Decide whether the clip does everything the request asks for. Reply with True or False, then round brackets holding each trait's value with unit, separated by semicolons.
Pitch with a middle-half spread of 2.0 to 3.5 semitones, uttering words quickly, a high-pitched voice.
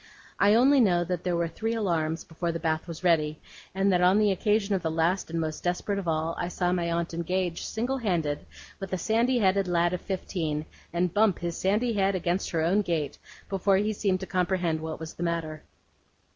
False (3.0 semitones; 215 wpm; 180 Hz)